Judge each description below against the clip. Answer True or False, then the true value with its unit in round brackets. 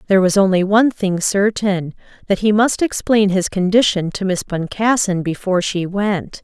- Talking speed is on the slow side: False (160 wpm)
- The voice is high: True (195 Hz)